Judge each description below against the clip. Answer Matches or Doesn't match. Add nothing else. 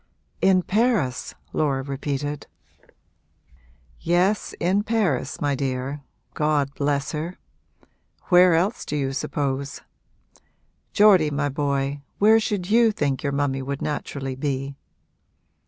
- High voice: Doesn't match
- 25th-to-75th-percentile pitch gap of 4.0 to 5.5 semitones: Matches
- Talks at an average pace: Doesn't match